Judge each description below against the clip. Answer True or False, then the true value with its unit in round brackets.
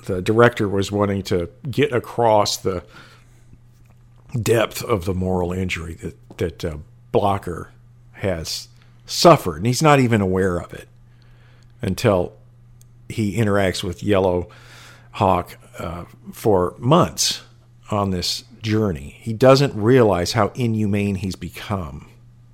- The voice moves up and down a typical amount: True (4.2 semitones)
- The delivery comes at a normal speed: False (120 wpm)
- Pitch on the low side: True (110 Hz)